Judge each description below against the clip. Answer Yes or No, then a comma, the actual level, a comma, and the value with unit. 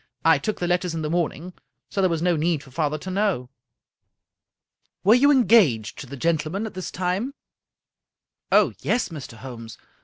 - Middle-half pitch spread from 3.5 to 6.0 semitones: Yes, average, 4.7 semitones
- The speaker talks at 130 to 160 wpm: No, average, 190 wpm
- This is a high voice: No, medium, 170 Hz